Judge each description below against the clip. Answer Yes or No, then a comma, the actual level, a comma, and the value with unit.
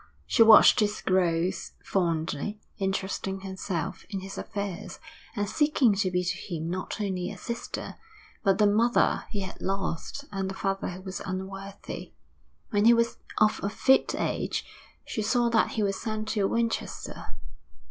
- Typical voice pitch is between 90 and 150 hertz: No, high, 195 Hz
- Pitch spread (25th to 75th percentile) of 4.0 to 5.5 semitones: No, narrow, 2.4 semitones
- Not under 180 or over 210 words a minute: No, average, 160 wpm